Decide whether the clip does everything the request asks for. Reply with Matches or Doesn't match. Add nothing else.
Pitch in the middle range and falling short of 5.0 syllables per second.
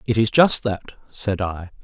Doesn't match